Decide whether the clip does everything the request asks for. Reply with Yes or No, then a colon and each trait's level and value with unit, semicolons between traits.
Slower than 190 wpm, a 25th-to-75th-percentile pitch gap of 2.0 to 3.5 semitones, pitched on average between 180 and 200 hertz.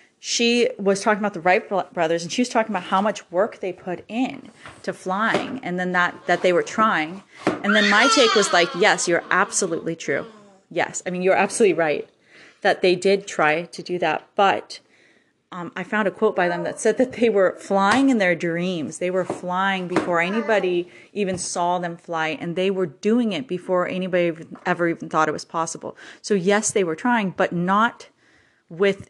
No: average, 200 wpm; average, 3.0 semitones; medium, 185 Hz